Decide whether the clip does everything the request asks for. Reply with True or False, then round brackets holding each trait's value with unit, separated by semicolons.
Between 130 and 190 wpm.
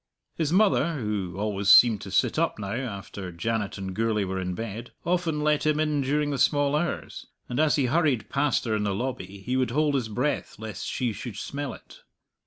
False (205 wpm)